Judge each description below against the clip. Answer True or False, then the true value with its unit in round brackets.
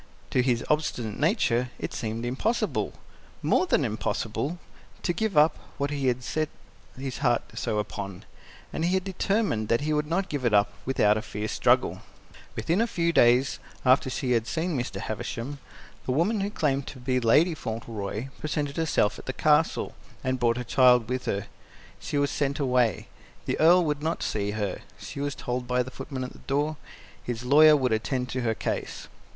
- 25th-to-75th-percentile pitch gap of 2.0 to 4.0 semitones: False (4.5 semitones)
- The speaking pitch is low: True (130 Hz)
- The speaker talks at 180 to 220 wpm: True (185 wpm)